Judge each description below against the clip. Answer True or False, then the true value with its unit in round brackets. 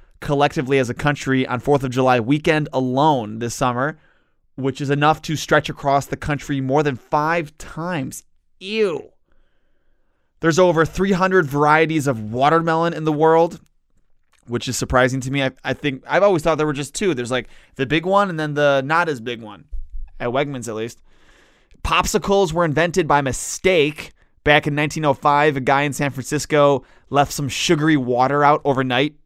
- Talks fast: False (170 wpm)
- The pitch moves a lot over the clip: False (3.2 semitones)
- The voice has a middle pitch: True (145 Hz)